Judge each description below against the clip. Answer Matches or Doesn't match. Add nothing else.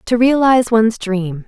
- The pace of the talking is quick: Doesn't match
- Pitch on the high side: Matches